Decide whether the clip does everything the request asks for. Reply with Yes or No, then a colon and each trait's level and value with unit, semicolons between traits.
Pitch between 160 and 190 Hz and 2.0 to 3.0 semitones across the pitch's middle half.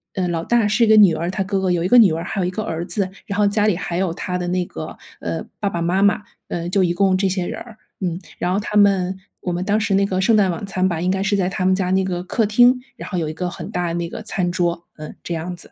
Yes: medium, 185 Hz; narrow, 2.4 semitones